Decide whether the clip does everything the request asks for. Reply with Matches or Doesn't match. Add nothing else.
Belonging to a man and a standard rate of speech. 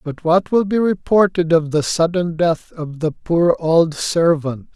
Matches